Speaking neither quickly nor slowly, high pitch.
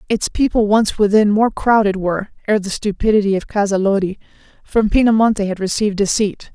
Yes: average, 155 wpm; high, 205 Hz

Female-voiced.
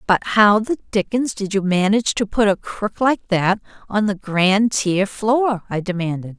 Yes: female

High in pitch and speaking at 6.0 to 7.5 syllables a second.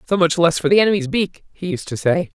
No: medium, 175 Hz; 6.3 syllables/s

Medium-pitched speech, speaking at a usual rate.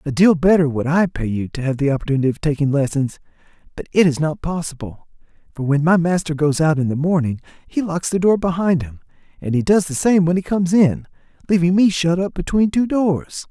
No: medium, 160 Hz; fast, 220 wpm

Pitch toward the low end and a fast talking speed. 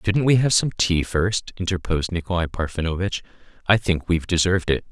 No: very low, 90 Hz; average, 170 wpm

